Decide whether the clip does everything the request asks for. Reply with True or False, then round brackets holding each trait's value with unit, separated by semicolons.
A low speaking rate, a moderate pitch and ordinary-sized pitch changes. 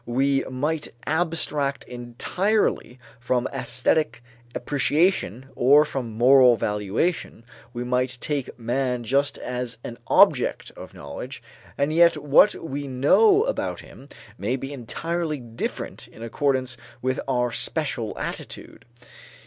False (115 wpm; 130 Hz; 3.5 semitones)